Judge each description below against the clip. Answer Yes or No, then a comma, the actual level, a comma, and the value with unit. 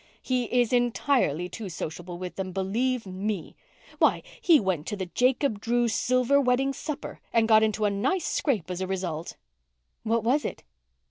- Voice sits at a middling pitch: No, high, 220 Hz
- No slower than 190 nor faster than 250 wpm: No, average, 170 wpm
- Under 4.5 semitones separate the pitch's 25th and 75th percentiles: No, average, 5.1 semitones